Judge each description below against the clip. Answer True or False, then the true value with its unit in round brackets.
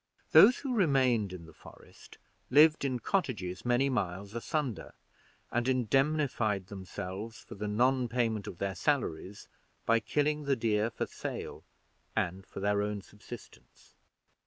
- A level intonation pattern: False (5.0 semitones)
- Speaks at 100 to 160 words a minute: True (135 wpm)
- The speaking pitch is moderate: False (115 Hz)